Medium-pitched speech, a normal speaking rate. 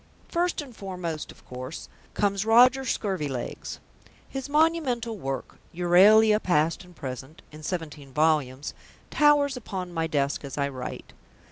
No: medium, 180 Hz; slow, 130 wpm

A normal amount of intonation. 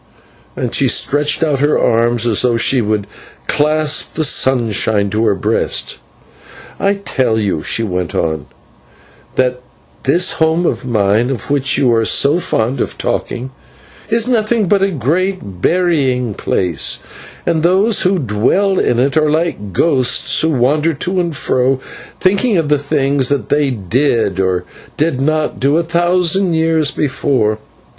No: wide, 6.1 semitones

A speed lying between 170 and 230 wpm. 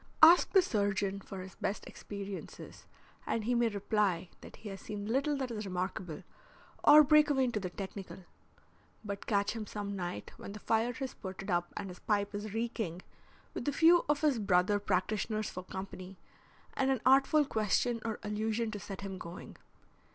Yes: average, 180 wpm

